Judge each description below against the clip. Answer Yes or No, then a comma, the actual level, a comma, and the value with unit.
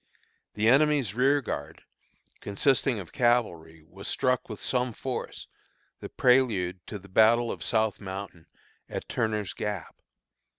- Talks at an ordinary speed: No, slow, 125 wpm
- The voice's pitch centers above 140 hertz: No, low, 110 Hz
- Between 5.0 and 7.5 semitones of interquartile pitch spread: No, average, 4.4 semitones